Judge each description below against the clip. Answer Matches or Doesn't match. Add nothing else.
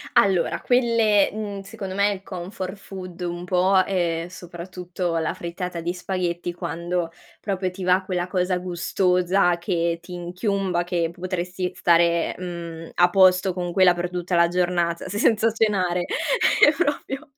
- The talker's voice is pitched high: Doesn't match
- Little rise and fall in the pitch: Matches